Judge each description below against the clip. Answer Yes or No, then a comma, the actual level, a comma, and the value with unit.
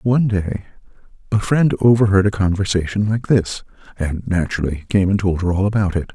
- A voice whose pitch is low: Yes, very low, 95 Hz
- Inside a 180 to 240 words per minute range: No, average, 165 wpm